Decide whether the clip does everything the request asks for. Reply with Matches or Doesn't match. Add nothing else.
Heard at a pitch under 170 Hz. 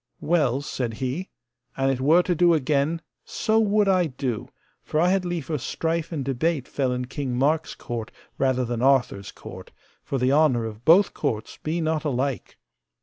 Matches